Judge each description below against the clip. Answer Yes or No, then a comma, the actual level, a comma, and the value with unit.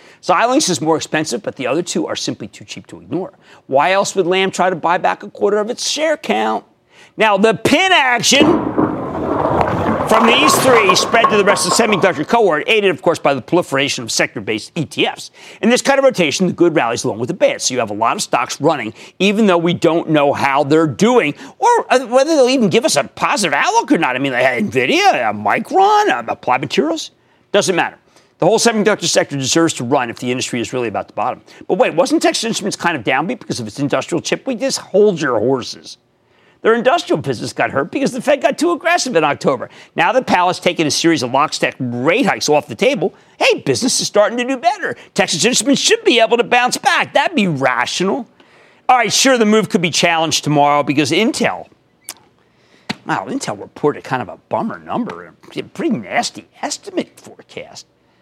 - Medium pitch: No, high, 195 Hz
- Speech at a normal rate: No, fast, 210 wpm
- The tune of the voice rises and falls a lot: Yes, wide, 8.7 semitones